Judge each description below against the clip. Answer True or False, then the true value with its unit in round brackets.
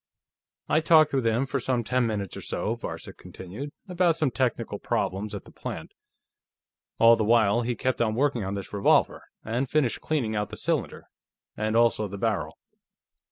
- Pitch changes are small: False (3.8 semitones)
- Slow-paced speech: False (175 wpm)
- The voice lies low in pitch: True (115 Hz)